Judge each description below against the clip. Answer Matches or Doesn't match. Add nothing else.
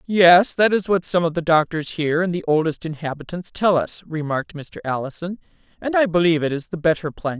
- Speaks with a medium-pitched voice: Matches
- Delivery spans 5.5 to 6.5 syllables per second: Matches